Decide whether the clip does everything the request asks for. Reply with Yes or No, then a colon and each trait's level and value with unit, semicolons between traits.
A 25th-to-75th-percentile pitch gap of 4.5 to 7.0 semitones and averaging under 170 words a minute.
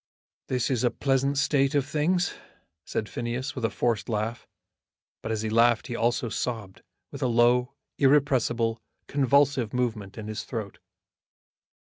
No: average, 3.3 semitones; average, 145 wpm